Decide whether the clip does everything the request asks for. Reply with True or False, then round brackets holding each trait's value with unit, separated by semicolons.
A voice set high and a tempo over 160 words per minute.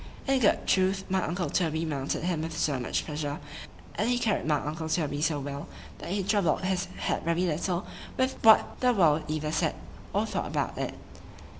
False (165 Hz; 185 wpm)